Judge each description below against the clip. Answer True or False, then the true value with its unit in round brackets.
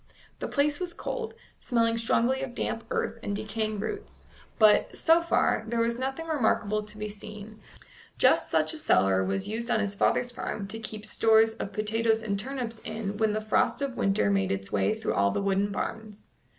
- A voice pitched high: True (220 Hz)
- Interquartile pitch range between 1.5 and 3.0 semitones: True (2.5 semitones)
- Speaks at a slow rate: False (190 wpm)